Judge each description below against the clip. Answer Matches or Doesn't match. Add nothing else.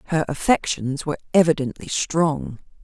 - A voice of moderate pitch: Matches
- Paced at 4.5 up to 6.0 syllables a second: Matches